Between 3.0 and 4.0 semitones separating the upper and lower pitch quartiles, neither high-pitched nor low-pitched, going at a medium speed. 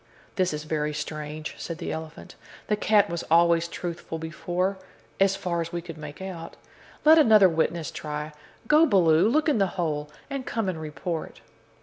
Yes: average, 3.7 semitones; medium, 170 Hz; average, 170 wpm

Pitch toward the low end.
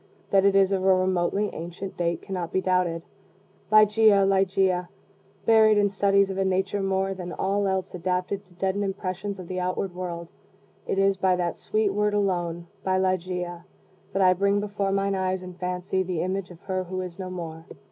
No: high, 190 Hz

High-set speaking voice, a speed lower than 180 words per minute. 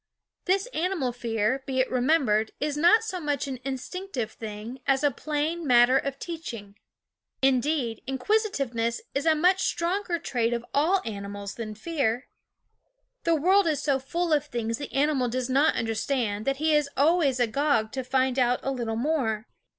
Yes: very high, 270 Hz; average, 165 wpm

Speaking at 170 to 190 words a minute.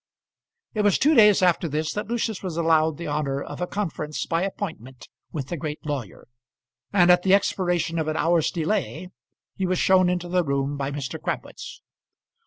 Yes: average, 185 wpm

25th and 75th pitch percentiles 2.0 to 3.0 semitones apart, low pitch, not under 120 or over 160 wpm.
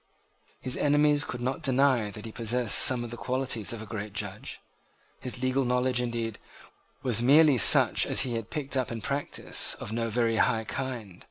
No: narrow, 2.6 semitones; low, 120 Hz; average, 185 wpm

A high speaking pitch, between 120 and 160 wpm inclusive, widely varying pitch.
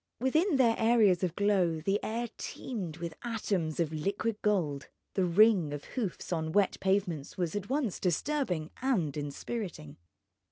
Yes: high, 195 Hz; average, 150 wpm; wide, 5.7 semitones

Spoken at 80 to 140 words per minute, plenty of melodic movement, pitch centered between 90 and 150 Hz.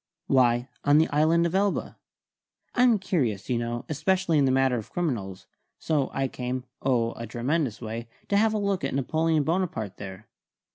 No: average, 175 wpm; wide, 6.0 semitones; low, 135 Hz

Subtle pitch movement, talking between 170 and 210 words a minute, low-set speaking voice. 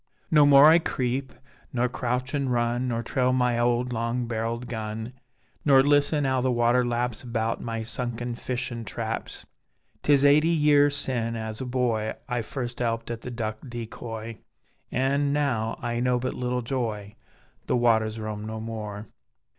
No: narrow, 2.3 semitones; average, 155 wpm; low, 120 Hz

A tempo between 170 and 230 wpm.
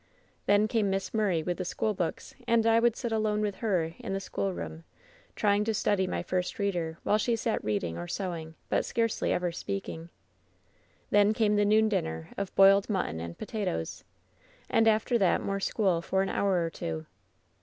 Yes: average, 185 wpm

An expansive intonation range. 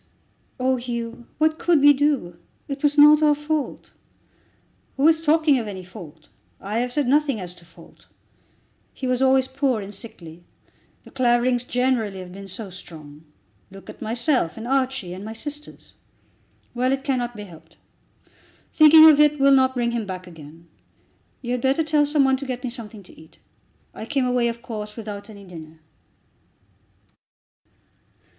Yes: wide, 5.8 semitones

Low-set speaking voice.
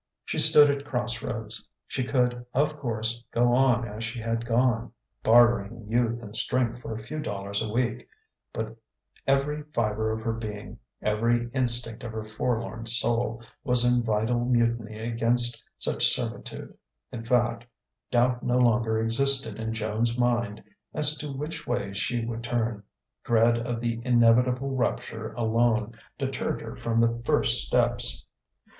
Yes: low, 120 Hz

